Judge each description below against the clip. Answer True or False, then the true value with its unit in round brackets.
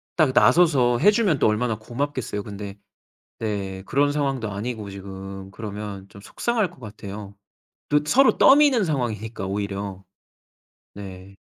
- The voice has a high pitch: False (110 Hz)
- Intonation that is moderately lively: False (6.2 semitones)